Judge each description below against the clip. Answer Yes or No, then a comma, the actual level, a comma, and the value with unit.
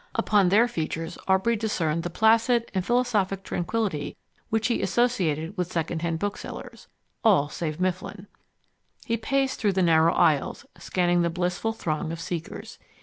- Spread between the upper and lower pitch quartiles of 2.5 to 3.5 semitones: No, average, 5.1 semitones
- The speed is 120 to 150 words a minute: Yes, average, 145 wpm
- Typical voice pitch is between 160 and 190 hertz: Yes, medium, 185 Hz